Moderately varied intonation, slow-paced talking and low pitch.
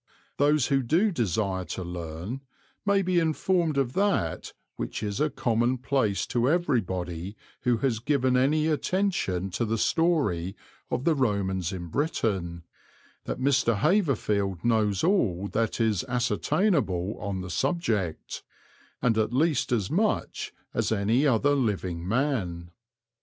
No: wide, 7.2 semitones; slow, 130 wpm; low, 115 Hz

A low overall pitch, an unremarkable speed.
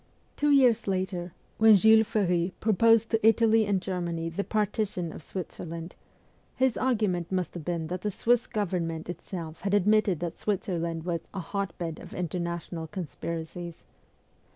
No: medium, 185 Hz; average, 150 wpm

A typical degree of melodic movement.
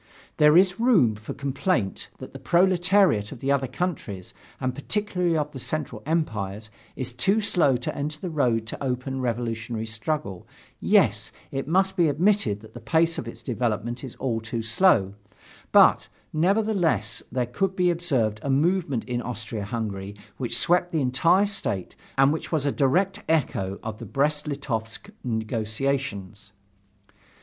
No: wide, 6.9 semitones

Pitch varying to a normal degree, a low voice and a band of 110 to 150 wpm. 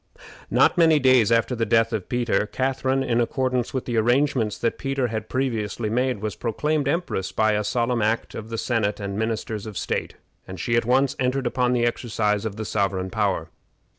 No: average, 3.2 semitones; low, 115 Hz; average, 195 wpm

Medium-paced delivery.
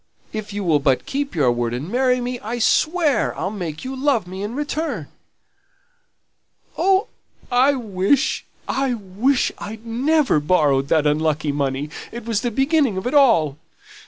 Yes: average, 160 wpm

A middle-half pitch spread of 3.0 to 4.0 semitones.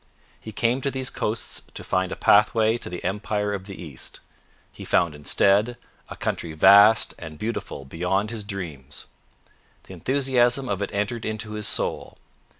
Yes: average, 3.7 semitones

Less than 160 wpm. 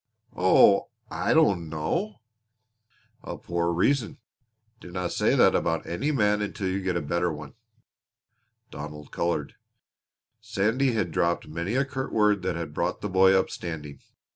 Yes: average, 145 wpm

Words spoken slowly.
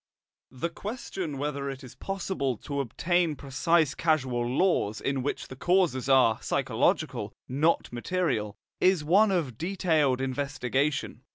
Yes: slow, 125 wpm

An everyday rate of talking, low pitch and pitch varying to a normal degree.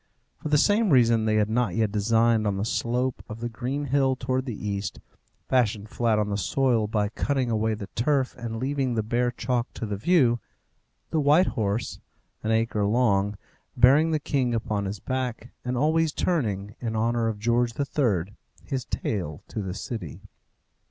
Yes: average, 180 wpm; low, 115 Hz; average, 3.5 semitones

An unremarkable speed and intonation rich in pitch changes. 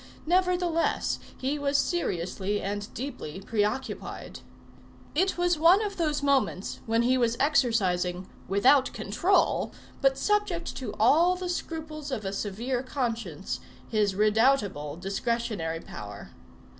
No: slow, 120 wpm; wide, 7.3 semitones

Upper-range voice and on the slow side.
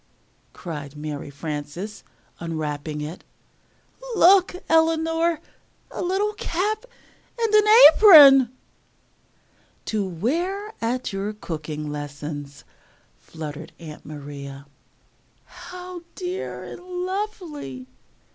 Yes: high, 210 Hz; slow, 80 wpm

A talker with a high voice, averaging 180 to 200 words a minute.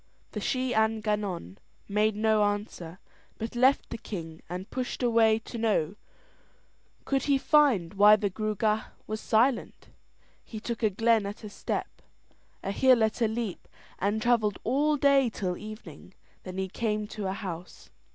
No: high, 215 Hz; average, 160 wpm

